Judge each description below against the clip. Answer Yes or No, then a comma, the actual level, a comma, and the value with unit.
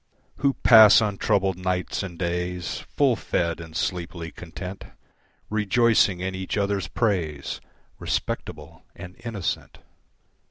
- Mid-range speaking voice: No, very low, 95 Hz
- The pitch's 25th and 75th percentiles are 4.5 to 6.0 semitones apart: No, average, 3.0 semitones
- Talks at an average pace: No, slow, 110 wpm